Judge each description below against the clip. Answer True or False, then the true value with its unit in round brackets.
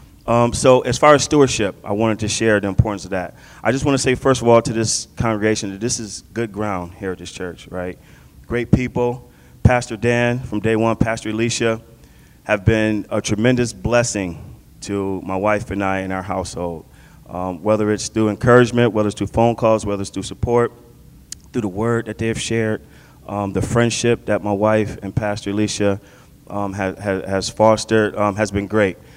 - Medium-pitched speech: False (110 Hz)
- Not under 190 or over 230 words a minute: True (195 wpm)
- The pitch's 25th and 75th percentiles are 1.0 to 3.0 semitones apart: True (2.7 semitones)